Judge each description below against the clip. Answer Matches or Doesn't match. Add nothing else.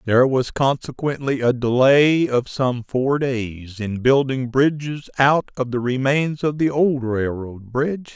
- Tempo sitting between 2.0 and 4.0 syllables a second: Matches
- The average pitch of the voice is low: Matches